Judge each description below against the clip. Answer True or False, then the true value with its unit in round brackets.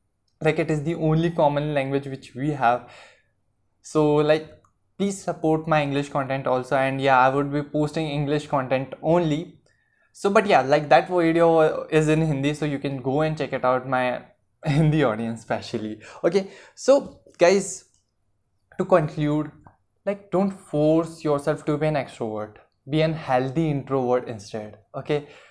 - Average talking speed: True (160 wpm)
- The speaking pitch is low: False (150 Hz)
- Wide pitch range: False (3.6 semitones)